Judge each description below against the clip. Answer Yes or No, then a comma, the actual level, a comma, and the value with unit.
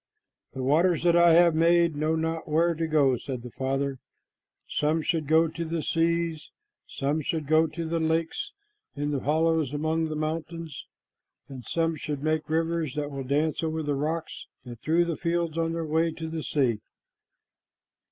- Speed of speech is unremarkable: Yes, average, 175 wpm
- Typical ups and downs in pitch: No, narrow, 2.0 semitones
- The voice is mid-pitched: Yes, medium, 160 Hz